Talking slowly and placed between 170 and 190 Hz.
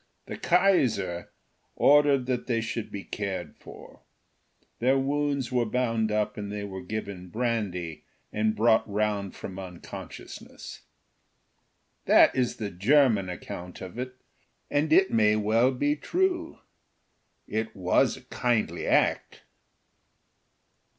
No: slow, 120 wpm; low, 110 Hz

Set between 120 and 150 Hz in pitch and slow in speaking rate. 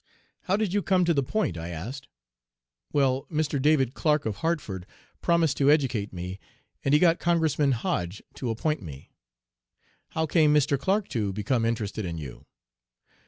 No: medium, 140 Hz; average, 165 wpm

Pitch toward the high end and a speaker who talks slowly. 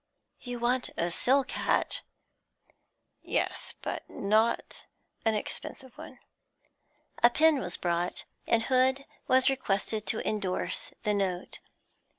Yes: high, 225 Hz; slow, 115 wpm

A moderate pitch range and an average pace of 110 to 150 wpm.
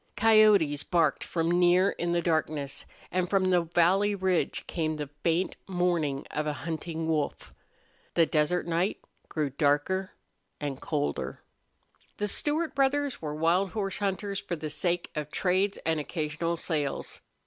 Yes: average, 3.7 semitones; average, 140 wpm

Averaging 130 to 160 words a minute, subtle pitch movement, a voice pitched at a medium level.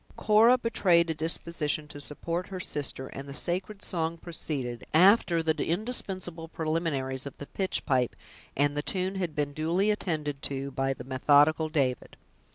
No: average, 155 wpm; average, 4.2 semitones; medium, 160 Hz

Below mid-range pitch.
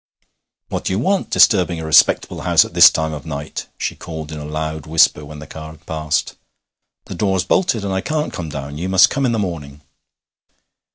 Yes: very low, 80 Hz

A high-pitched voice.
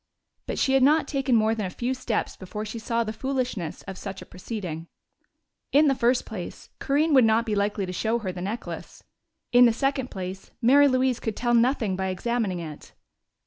Yes: high, 230 Hz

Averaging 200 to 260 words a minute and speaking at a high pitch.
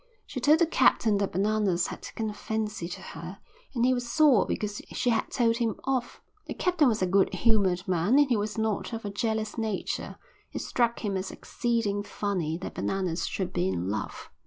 Yes: fast, 205 wpm; high, 215 Hz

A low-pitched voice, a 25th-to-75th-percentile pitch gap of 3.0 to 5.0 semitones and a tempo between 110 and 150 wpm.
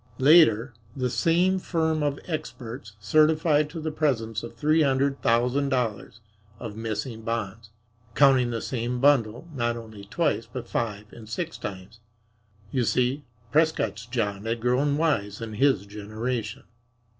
Yes: low, 120 Hz; average, 4.6 semitones; average, 140 wpm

